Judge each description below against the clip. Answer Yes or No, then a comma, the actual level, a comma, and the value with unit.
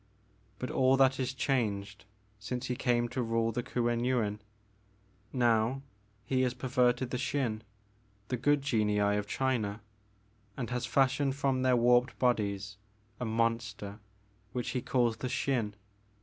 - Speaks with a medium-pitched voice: No, low, 120 Hz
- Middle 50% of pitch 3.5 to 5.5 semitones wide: No, average, 3.1 semitones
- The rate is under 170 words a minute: Yes, average, 150 wpm